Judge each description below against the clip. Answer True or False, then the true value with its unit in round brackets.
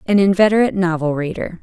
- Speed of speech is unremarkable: True (150 wpm)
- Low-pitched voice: False (185 Hz)